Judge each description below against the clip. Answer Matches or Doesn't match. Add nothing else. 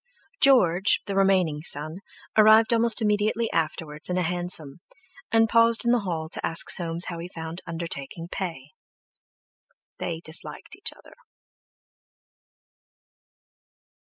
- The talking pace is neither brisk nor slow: Doesn't match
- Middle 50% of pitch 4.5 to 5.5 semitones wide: Matches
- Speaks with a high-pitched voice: Doesn't match